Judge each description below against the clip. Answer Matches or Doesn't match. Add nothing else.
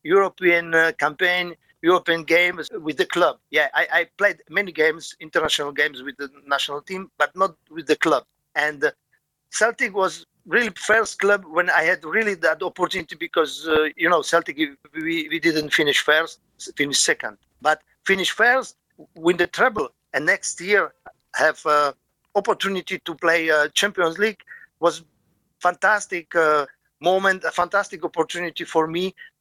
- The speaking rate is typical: Matches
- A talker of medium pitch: Matches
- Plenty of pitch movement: Doesn't match